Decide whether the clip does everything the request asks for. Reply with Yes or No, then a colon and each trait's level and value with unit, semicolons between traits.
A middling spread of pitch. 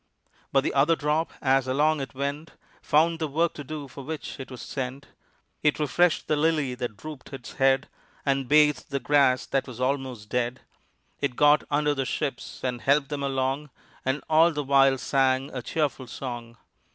No: narrow, 2.3 semitones